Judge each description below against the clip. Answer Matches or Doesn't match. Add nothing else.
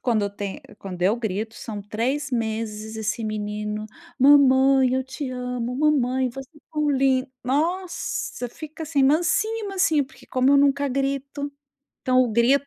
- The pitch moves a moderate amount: Matches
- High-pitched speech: Matches